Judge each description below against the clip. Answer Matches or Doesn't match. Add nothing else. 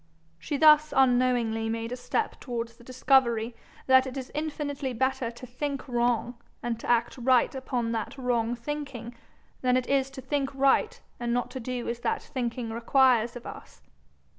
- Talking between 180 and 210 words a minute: Doesn't match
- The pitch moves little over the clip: Matches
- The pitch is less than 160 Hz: Doesn't match